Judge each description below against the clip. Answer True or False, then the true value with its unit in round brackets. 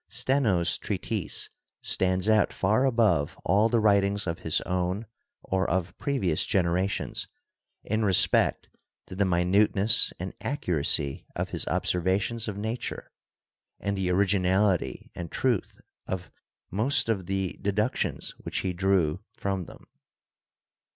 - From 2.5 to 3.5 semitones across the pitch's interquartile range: True (2.9 semitones)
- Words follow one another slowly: True (125 wpm)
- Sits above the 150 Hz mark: False (95 Hz)